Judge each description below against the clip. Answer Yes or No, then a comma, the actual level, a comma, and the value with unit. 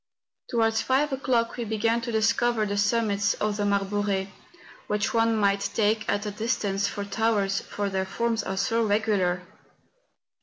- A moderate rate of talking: Yes, average, 160 wpm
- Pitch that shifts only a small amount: Yes, narrow, 2.2 semitones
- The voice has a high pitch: Yes, high, 210 Hz